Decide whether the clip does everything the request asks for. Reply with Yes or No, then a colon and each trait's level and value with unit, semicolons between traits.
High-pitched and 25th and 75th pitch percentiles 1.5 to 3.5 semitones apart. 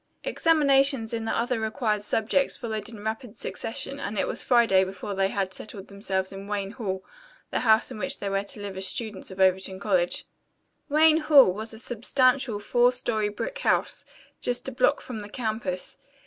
No: high, 220 Hz; average, 4.0 semitones